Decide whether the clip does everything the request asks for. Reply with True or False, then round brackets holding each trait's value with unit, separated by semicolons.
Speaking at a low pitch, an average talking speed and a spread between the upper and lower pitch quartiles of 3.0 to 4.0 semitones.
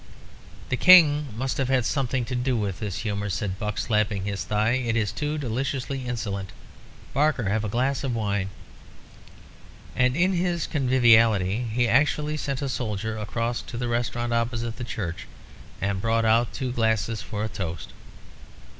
True (115 Hz; 160 wpm; 3.6 semitones)